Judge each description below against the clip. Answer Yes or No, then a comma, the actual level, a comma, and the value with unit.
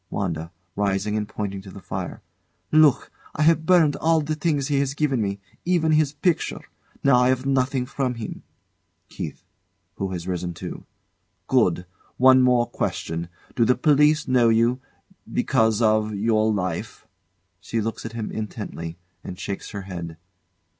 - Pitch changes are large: Yes, wide, 5.7 semitones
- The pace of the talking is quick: No, average, 155 wpm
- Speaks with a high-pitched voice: No, low, 115 Hz